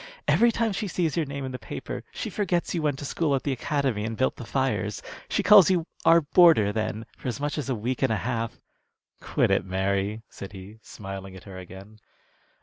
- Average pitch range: No, wide, 6.9 semitones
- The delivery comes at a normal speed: No, fast, 220 wpm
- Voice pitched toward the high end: No, low, 125 Hz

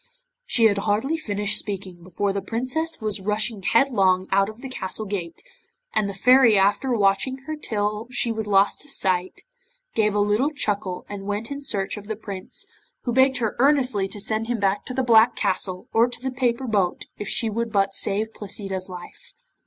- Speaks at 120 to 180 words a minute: No, average, 190 wpm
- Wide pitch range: No, average, 3.6 semitones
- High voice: Yes, high, 210 Hz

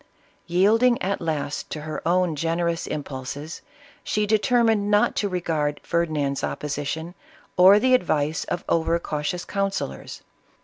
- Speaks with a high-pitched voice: No, medium, 170 Hz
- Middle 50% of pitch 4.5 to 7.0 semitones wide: Yes, average, 4.9 semitones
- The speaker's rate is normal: No, slow, 125 wpm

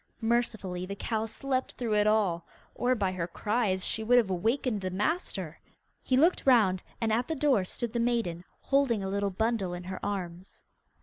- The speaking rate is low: No, average, 185 wpm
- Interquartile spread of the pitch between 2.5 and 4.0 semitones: No, average, 4.4 semitones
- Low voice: No, high, 215 Hz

